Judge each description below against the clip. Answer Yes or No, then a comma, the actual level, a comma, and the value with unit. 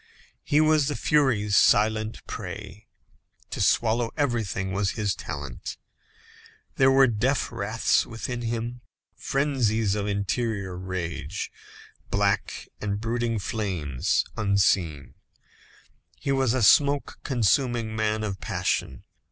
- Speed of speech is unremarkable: No, slow, 110 wpm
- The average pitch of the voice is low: Yes, low, 110 Hz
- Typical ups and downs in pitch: Yes, average, 3.6 semitones